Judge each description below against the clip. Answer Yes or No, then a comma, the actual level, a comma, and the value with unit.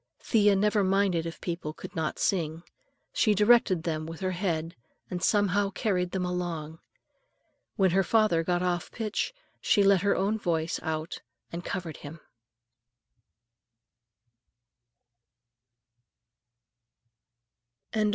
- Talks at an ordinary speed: No, slow, 115 wpm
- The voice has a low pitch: No, medium, 180 Hz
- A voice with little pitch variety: No, average, 3.4 semitones